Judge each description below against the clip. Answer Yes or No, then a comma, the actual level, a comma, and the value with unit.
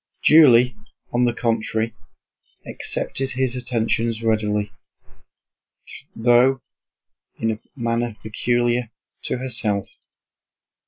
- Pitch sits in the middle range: No, low, 120 Hz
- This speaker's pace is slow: Yes, slow, 85 wpm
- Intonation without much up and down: Yes, narrow, 1.9 semitones